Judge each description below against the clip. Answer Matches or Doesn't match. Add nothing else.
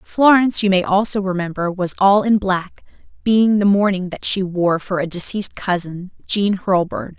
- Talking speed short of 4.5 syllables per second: Doesn't match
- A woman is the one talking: Matches